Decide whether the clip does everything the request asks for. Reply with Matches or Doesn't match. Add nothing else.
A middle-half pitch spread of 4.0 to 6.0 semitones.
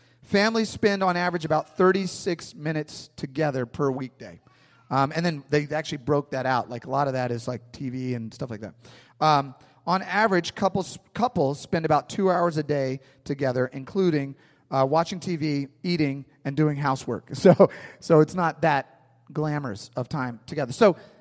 Matches